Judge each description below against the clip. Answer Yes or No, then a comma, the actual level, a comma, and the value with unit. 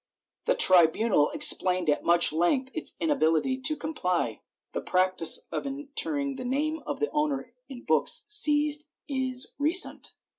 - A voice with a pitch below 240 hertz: No, very high, 265 Hz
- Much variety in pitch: Yes, wide, 8.4 semitones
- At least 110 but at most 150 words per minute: Yes, average, 140 wpm